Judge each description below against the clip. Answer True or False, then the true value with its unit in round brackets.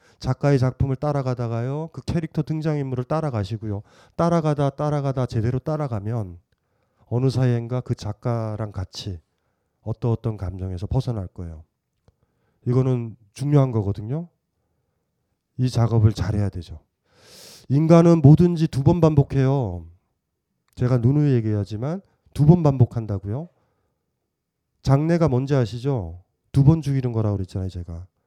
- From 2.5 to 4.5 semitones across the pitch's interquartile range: False (5.2 semitones)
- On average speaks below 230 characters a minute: False (295 characters per minute)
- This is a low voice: True (125 Hz)